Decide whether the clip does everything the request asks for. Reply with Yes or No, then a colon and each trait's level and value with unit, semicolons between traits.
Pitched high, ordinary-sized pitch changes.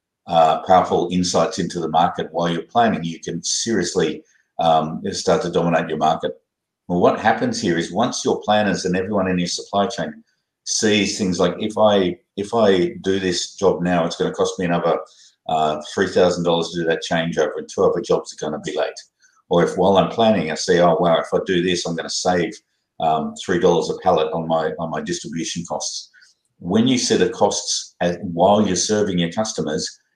No: very low, 90 Hz; average, 3.2 semitones